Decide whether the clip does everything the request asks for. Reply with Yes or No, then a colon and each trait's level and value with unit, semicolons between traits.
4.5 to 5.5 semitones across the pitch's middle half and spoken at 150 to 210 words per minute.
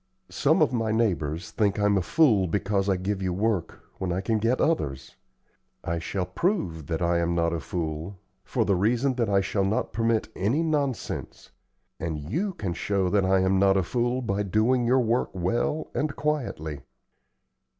Yes: average, 5.0 semitones; average, 180 wpm